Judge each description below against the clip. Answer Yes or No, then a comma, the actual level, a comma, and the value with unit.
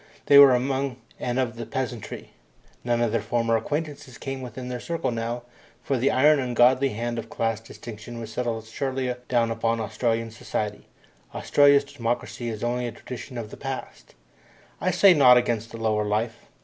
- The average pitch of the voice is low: Yes, low, 120 Hz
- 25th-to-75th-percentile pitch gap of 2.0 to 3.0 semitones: Yes, narrow, 2.4 semitones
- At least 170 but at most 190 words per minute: Yes, average, 175 wpm